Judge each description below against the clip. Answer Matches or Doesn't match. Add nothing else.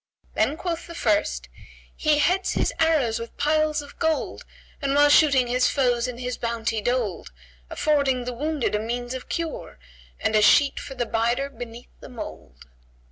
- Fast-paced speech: Doesn't match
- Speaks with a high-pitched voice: Matches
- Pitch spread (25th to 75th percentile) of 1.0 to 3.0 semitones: Doesn't match